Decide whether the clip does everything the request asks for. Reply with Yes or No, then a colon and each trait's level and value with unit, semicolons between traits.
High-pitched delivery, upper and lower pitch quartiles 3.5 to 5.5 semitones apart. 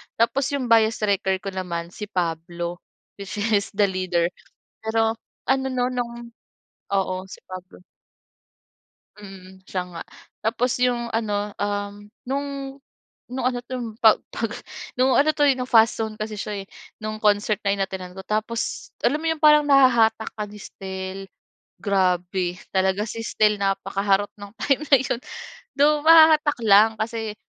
Yes: high, 215 Hz; average, 3.9 semitones